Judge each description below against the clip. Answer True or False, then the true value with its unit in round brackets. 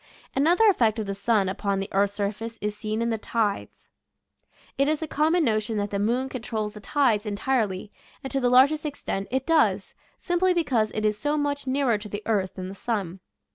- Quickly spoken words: True (210 wpm)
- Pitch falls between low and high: False (225 Hz)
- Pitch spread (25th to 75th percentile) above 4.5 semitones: True (5.1 semitones)